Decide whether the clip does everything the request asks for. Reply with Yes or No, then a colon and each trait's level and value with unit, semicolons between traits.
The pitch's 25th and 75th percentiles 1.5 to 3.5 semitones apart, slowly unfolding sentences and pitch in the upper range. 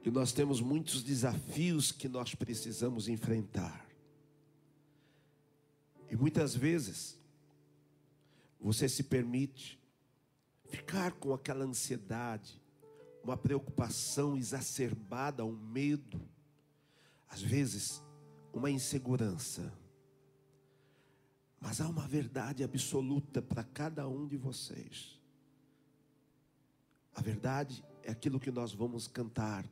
No: average, 3.1 semitones; slow, 95 wpm; low, 135 Hz